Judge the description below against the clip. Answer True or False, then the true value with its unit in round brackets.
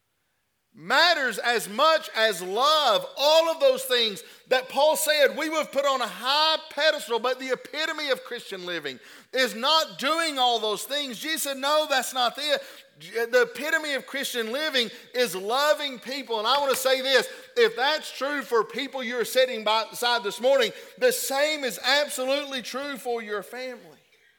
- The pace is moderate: True (175 wpm)